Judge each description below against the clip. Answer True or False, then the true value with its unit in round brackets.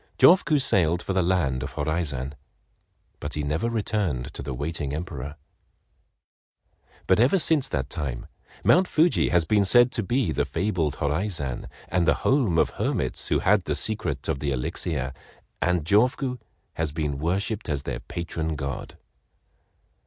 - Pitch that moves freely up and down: True (6.6 semitones)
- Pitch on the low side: True (85 Hz)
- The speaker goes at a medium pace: True (150 wpm)